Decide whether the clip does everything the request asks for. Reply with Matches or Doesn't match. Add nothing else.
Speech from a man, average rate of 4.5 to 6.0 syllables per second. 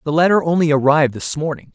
Doesn't match